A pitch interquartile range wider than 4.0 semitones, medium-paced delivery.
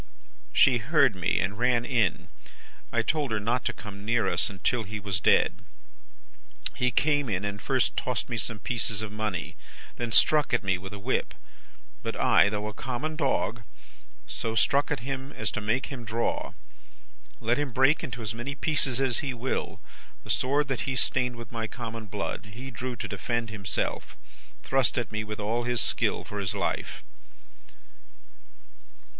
No: average, 3.6 semitones; average, 175 wpm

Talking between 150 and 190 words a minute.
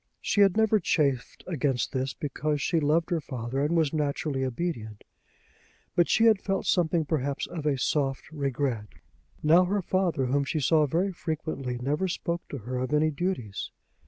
Yes: average, 170 wpm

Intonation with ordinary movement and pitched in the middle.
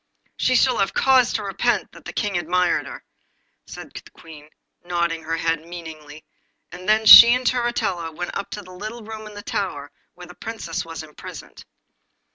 Yes: average, 4.8 semitones; medium, 180 Hz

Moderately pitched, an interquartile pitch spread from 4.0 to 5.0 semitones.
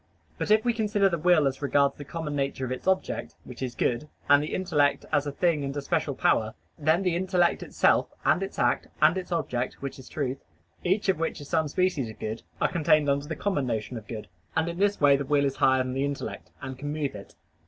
Yes: medium, 145 Hz; average, 4.3 semitones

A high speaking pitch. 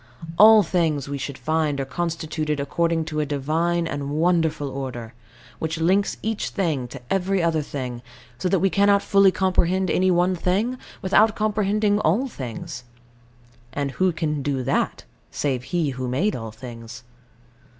No: medium, 160 Hz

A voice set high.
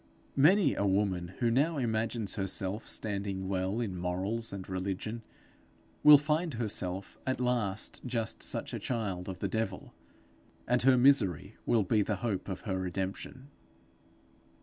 No: low, 105 Hz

